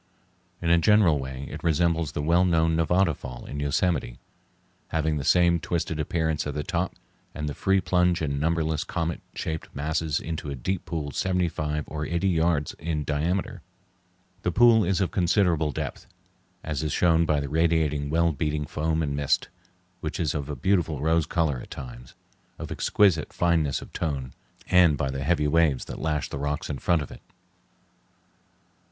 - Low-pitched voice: Yes, very low, 80 Hz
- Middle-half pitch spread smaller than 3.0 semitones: Yes, narrow, 2.6 semitones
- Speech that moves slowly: No, average, 175 wpm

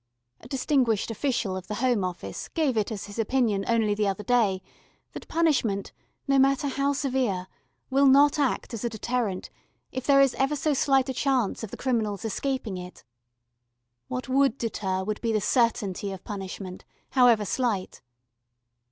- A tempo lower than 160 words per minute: No, average, 165 wpm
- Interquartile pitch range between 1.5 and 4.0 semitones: No, average, 4.8 semitones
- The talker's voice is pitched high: Yes, high, 235 Hz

